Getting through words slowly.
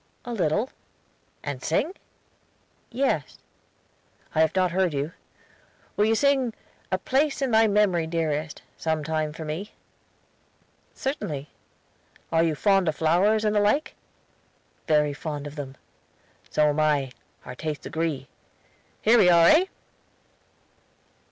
Yes: slow, 130 wpm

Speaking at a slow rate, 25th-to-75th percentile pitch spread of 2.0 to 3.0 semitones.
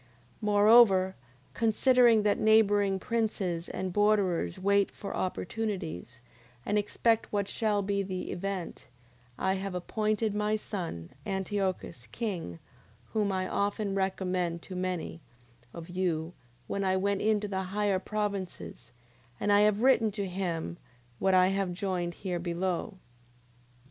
Yes: slow, 130 wpm; narrow, 2.4 semitones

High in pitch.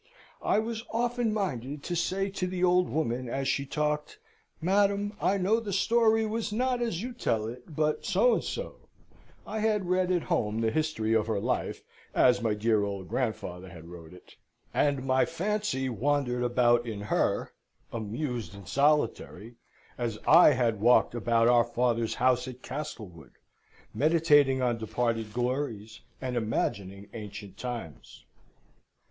No: low, 130 Hz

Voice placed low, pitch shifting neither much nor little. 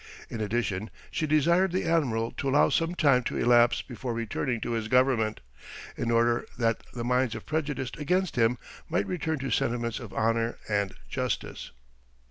Yes: low, 120 Hz; average, 4.2 semitones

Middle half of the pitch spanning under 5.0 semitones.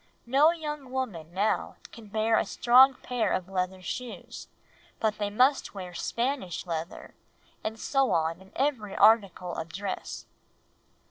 No: wide, 5.5 semitones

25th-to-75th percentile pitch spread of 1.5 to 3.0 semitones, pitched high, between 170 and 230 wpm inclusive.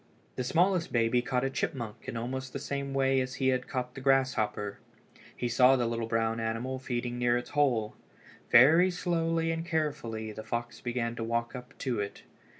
No: average, 2.7 semitones; low, 125 Hz; average, 185 wpm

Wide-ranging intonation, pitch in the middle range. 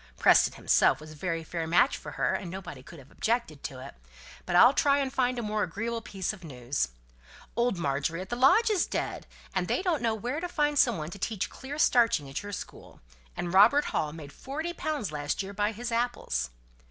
No: wide, 7.4 semitones; high, 205 Hz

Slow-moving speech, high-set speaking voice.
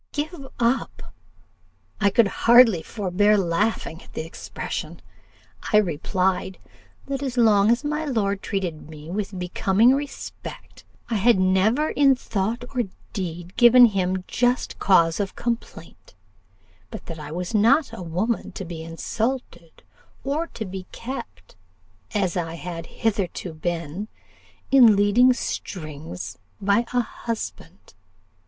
Yes: slow, 130 wpm; high, 205 Hz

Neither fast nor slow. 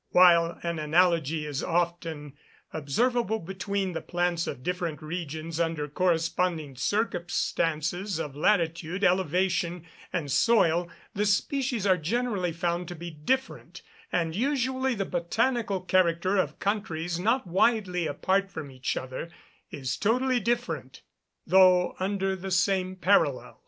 No: slow, 125 wpm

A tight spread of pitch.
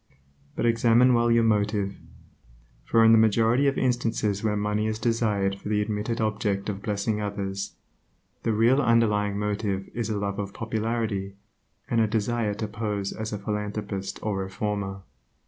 Yes: narrow, 2.0 semitones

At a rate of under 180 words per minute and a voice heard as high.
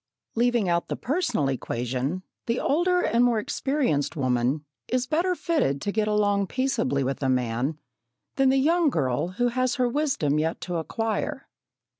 Yes: average, 160 wpm; high, 210 Hz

